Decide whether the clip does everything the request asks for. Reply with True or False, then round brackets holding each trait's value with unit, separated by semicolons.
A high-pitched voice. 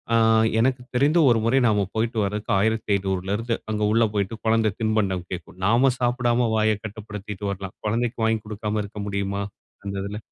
False (110 Hz)